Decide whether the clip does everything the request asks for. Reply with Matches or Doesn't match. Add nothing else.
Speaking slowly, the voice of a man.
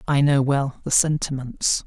Doesn't match